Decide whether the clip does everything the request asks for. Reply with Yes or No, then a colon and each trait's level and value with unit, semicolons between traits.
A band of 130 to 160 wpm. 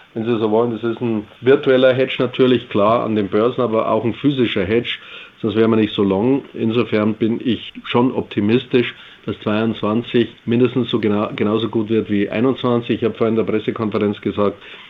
No: fast, 190 wpm